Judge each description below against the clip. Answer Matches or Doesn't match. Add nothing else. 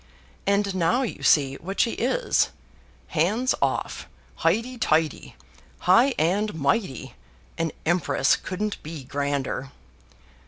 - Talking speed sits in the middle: Doesn't match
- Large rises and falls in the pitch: Matches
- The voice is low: Doesn't match